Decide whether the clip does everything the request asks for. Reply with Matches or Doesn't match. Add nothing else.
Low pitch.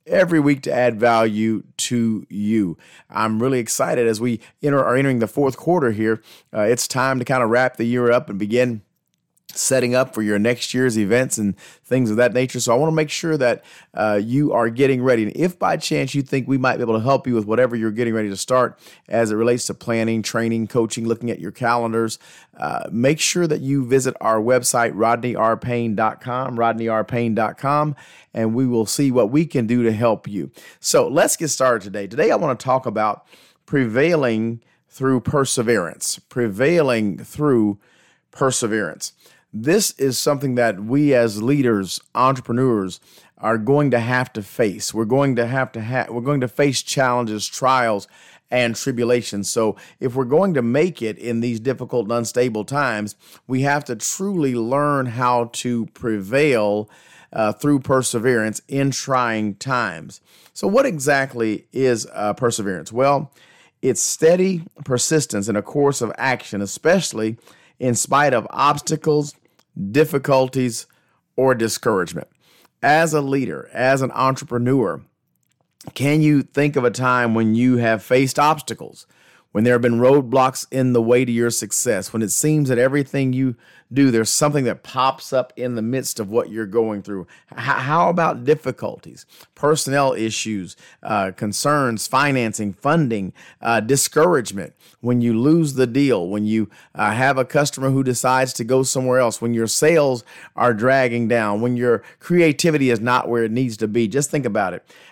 Matches